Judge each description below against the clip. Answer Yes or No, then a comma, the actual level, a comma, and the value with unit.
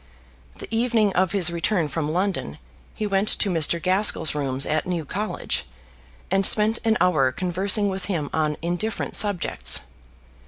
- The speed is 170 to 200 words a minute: No, average, 150 wpm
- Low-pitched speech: No, medium, 185 Hz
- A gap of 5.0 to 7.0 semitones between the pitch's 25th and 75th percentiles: No, average, 4.1 semitones